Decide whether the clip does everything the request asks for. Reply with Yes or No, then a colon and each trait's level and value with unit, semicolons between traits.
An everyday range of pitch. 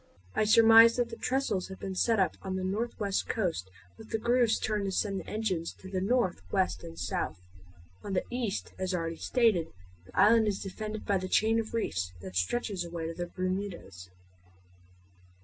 Yes: average, 4.0 semitones